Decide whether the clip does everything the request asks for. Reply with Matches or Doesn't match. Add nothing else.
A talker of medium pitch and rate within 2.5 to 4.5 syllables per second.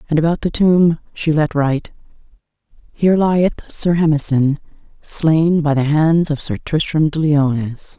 Matches